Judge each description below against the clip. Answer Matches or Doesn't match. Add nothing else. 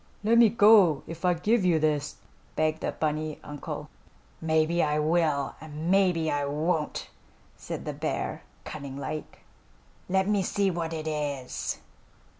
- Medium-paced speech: Matches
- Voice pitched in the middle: Matches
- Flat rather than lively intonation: Doesn't match